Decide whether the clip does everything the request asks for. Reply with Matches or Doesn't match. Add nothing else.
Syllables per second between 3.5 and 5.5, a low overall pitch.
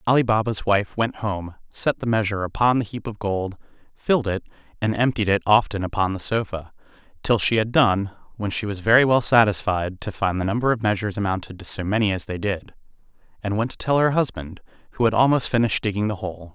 Doesn't match